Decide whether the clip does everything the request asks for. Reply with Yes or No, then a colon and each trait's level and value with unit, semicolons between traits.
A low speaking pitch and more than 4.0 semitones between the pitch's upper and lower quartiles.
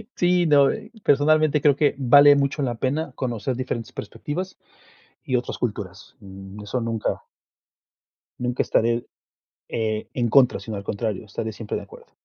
Yes: low, 125 Hz; average, 4.7 semitones